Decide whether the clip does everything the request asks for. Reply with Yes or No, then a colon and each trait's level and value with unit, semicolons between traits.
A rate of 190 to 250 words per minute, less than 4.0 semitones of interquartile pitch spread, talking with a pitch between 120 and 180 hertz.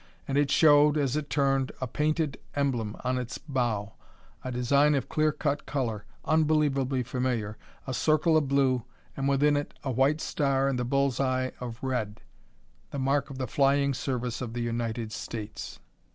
No: average, 170 wpm; narrow, 2.6 semitones; low, 135 Hz